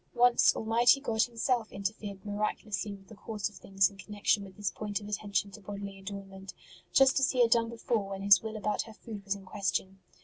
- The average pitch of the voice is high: Yes, high, 205 Hz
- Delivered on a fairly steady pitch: Yes, narrow, 2.3 semitones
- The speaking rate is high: Yes, fast, 210 wpm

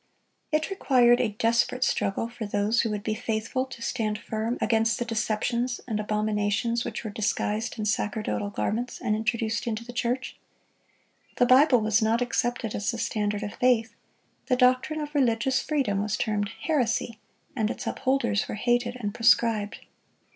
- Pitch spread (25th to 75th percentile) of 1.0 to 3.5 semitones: Yes, narrow, 2.5 semitones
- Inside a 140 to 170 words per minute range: Yes, average, 160 wpm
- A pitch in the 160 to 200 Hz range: No, high, 230 Hz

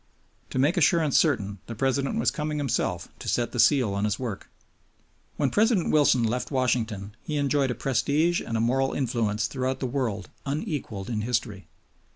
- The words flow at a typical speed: Yes, average, 175 wpm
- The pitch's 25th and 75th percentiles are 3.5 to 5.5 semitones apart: Yes, average, 4.5 semitones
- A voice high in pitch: No, low, 130 Hz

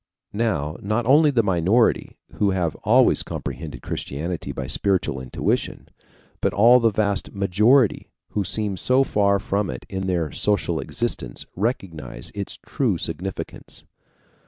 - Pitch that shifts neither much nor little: Yes, average, 4.2 semitones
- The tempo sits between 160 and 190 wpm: No, slow, 135 wpm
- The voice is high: No, low, 100 Hz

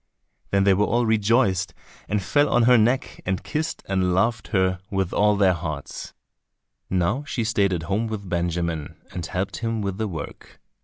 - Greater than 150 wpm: Yes, average, 175 wpm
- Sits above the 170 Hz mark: No, low, 100 Hz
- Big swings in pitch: No, average, 3.7 semitones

